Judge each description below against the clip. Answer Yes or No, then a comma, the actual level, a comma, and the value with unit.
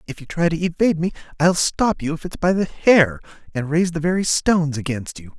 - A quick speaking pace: Yes, fast, 235 wpm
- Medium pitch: Yes, medium, 160 Hz